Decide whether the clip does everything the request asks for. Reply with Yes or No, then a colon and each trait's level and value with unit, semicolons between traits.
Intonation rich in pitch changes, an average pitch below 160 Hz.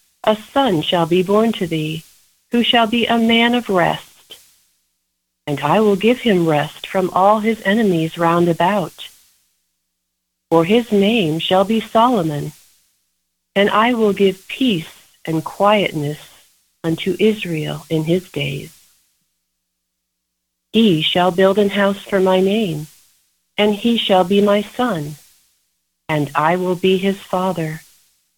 No: wide, 5.7 semitones; medium, 180 Hz